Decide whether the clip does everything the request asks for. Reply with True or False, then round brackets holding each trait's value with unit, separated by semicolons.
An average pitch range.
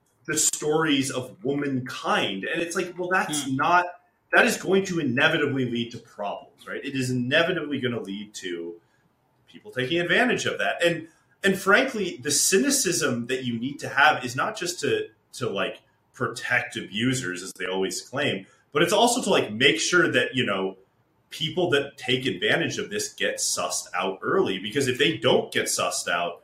False (5.8 semitones)